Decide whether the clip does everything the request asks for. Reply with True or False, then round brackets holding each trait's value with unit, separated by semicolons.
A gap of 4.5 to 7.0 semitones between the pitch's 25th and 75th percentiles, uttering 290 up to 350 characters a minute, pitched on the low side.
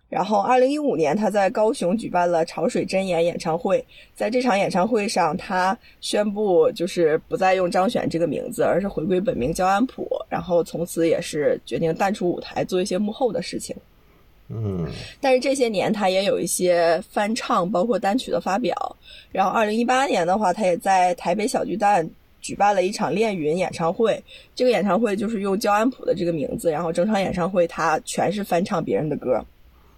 False (5.3 semitones; 300 characters per minute; 190 Hz)